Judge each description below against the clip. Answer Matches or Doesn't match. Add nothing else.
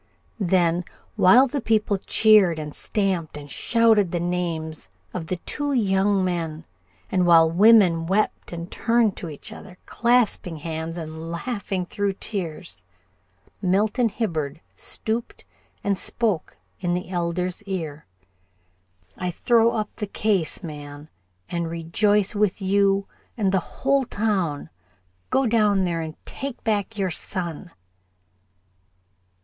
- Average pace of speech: Doesn't match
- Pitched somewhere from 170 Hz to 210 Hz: Matches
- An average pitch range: Matches